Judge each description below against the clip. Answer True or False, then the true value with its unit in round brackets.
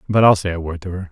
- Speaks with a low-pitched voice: True (90 Hz)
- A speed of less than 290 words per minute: False (380 wpm)